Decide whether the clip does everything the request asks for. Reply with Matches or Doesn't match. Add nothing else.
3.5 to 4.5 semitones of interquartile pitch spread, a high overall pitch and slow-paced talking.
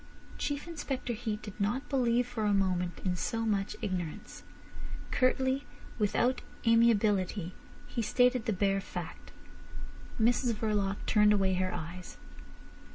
Matches